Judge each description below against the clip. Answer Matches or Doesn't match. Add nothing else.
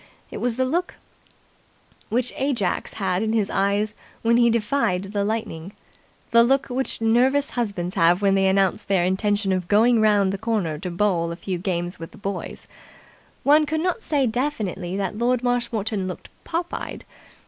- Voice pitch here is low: Doesn't match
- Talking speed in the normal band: Matches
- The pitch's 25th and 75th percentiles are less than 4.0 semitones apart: Doesn't match